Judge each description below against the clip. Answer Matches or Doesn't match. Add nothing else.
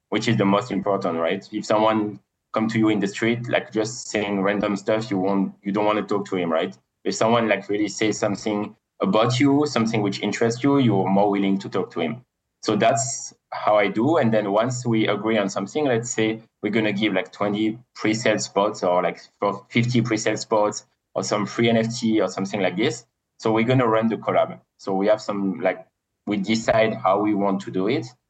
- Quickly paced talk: Matches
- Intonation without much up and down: Matches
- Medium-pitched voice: Doesn't match